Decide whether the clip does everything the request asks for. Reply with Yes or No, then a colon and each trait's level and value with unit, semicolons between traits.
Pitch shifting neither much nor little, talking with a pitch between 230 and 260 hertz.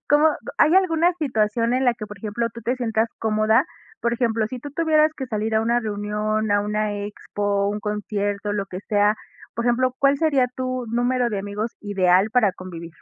No: average, 3.4 semitones; high, 220 Hz